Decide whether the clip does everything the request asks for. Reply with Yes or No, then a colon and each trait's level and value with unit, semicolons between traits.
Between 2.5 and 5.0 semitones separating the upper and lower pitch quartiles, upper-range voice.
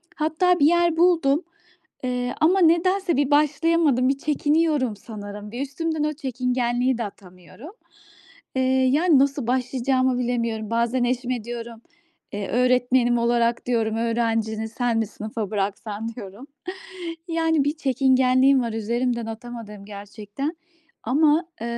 Yes: average, 4.3 semitones; very high, 250 Hz